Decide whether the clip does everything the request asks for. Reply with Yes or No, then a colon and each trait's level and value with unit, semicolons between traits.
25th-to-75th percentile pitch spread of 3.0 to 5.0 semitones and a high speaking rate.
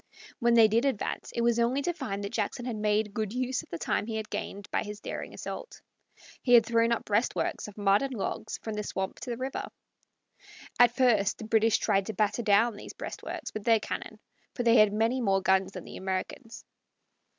No: narrow, 2.6 semitones; fast, 215 wpm